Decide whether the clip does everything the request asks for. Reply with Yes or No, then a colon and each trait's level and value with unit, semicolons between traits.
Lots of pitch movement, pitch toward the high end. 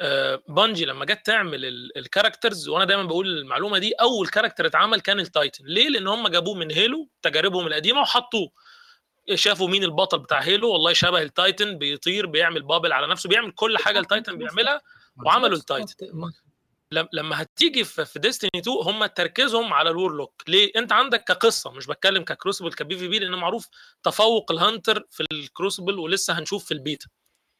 Yes: wide, 5.9 semitones; high, 195 Hz